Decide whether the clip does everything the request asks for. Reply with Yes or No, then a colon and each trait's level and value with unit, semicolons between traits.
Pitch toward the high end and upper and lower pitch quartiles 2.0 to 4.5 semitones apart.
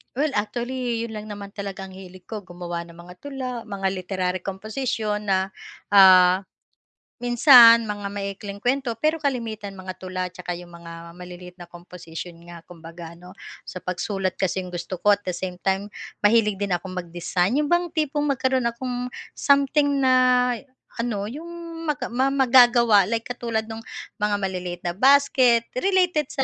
No: high, 205 Hz; wide, 5.4 semitones